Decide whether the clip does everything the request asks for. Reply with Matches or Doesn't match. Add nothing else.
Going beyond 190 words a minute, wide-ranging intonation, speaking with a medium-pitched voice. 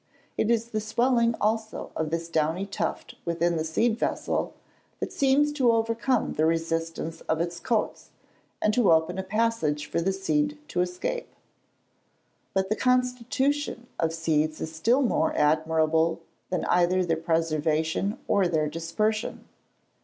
Doesn't match